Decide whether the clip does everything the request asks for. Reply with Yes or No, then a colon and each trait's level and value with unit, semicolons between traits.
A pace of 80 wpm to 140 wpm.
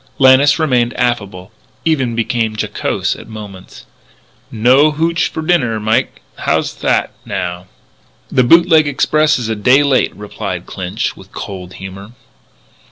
Yes: slow, 135 wpm